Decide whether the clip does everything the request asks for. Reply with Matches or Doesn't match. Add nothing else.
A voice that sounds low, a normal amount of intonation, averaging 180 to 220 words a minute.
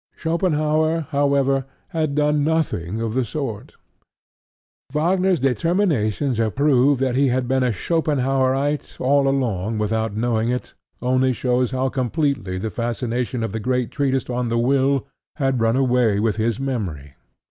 Doesn't match